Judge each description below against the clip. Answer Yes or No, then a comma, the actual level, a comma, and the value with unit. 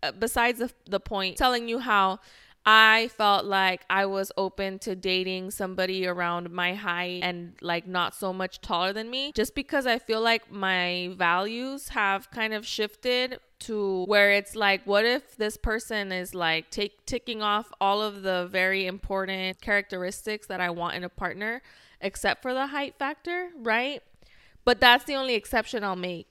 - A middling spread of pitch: Yes, average, 3.7 semitones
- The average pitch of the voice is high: Yes, high, 200 Hz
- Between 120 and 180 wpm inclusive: Yes, average, 175 wpm